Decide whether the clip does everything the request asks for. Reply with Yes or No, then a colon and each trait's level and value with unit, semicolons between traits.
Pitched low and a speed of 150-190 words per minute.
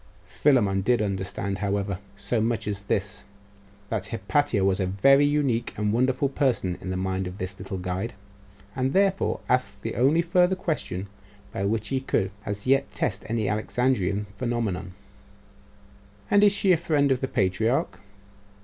Yes: low, 110 Hz; average, 160 wpm